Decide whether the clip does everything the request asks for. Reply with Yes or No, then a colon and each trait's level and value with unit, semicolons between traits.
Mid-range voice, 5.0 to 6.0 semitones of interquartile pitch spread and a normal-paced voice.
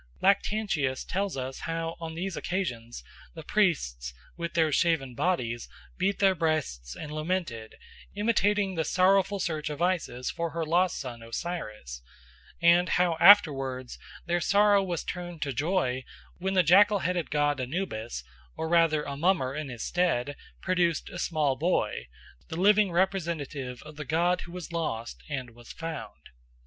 Yes: medium, 165 Hz; average, 5.3 semitones; average, 150 wpm